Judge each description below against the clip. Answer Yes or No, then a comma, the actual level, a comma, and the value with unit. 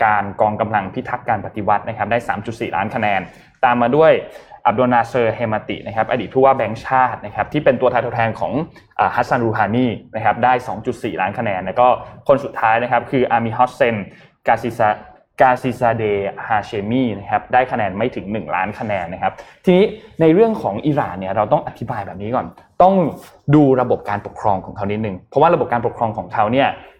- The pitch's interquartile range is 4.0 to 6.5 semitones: No, average, 3.3 semitones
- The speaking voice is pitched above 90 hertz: Yes, low, 120 Hz